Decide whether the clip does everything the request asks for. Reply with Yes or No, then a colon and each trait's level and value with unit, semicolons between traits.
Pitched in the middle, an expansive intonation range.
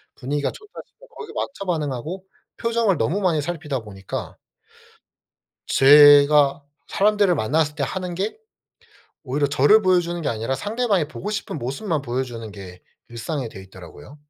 Yes: medium, 150 Hz; wide, 6.5 semitones